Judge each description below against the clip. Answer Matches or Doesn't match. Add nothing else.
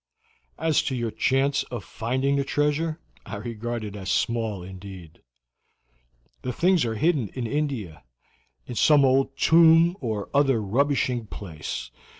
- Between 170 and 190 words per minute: Doesn't match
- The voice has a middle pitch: Doesn't match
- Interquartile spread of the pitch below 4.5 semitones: Doesn't match